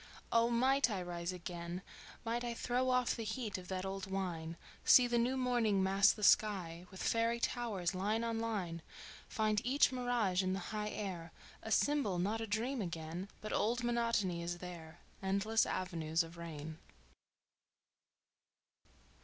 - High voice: Yes, high, 200 Hz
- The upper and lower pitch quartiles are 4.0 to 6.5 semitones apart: Yes, average, 4.8 semitones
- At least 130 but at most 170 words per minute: Yes, average, 155 wpm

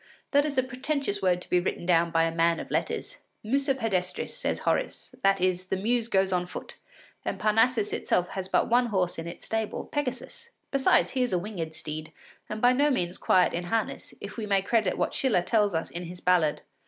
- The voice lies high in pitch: Yes, high, 195 Hz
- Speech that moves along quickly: Yes, fast, 215 wpm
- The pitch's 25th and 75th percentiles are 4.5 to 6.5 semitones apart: Yes, wide, 5.5 semitones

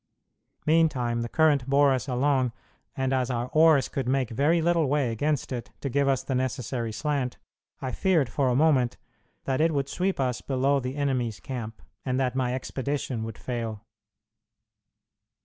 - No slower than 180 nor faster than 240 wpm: No, average, 165 wpm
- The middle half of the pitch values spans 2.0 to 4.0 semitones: Yes, narrow, 2.6 semitones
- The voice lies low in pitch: Yes, low, 130 Hz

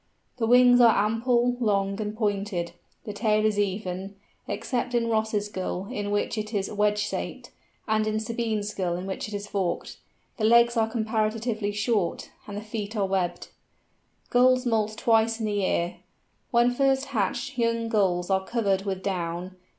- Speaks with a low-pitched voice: No, high, 215 Hz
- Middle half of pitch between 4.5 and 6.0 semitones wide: No, narrow, 2.6 semitones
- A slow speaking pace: No, average, 165 wpm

